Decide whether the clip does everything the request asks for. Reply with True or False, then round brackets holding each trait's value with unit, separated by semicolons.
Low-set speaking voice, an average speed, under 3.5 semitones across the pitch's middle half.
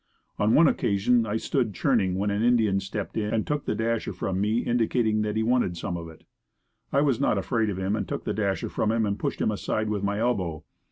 False (105 Hz; 235 wpm; 2.8 semitones)